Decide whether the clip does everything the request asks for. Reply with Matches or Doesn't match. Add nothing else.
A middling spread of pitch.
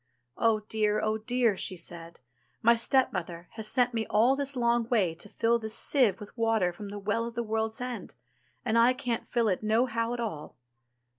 Doesn't match